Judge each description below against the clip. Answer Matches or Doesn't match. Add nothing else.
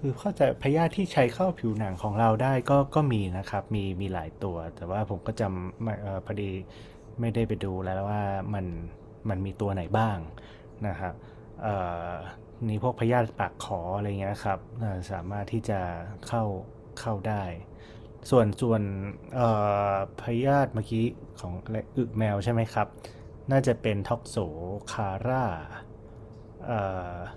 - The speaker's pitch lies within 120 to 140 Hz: Doesn't match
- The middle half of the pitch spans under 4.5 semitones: Matches